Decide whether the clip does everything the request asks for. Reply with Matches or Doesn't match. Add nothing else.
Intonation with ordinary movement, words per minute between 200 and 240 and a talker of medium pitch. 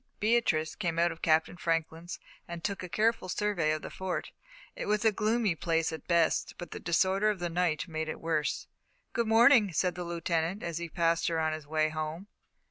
Matches